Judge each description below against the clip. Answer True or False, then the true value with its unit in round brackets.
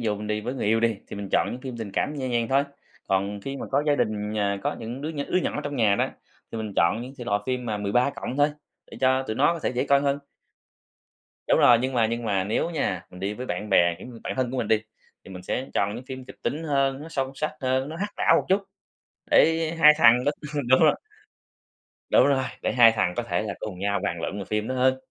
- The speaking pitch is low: True (120 Hz)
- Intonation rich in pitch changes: False (4.7 semitones)